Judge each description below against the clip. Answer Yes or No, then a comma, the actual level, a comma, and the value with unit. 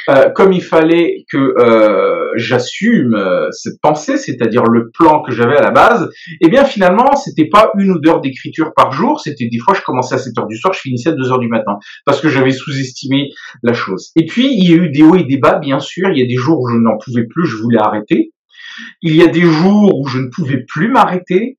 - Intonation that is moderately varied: No, wide, 7.1 semitones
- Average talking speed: No, fast, 250 wpm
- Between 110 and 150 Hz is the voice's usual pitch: No, medium, 160 Hz